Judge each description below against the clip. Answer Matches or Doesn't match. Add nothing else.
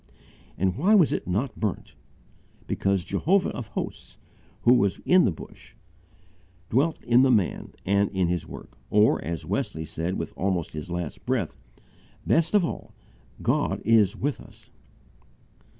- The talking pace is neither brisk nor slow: Matches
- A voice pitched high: Doesn't match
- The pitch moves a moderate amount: Doesn't match